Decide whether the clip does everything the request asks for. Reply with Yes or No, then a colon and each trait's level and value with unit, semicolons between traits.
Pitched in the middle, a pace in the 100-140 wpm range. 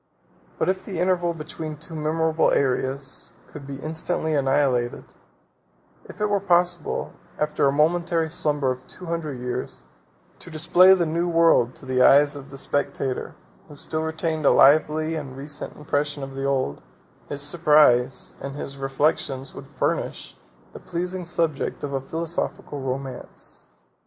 No: medium, 150 Hz; average, 150 wpm